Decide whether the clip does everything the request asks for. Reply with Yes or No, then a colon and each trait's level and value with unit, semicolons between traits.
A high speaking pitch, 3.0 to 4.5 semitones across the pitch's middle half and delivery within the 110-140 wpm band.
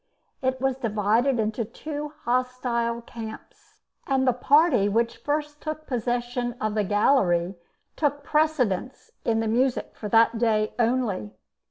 Yes: high, 240 Hz; average, 3.5 semitones; slow, 135 wpm